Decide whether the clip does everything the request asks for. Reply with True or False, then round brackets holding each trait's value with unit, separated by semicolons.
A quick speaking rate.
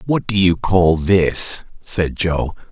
False (155 wpm)